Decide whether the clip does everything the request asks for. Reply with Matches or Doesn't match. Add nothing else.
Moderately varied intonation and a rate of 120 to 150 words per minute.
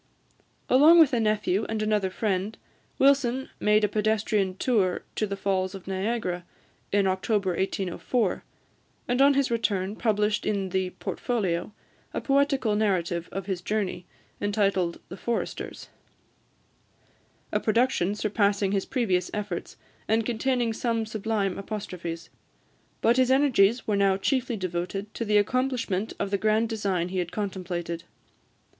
Matches